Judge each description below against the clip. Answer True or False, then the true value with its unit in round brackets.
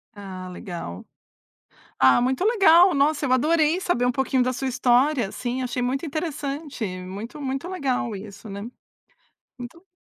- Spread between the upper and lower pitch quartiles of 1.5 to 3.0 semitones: False (4.8 semitones)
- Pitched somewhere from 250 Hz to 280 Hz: True (260 Hz)